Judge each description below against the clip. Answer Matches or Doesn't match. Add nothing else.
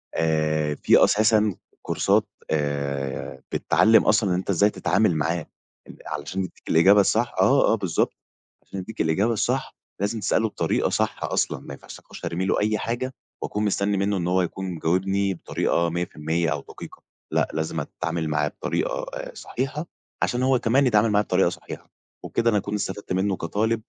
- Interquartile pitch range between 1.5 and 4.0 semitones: Doesn't match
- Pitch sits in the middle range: Doesn't match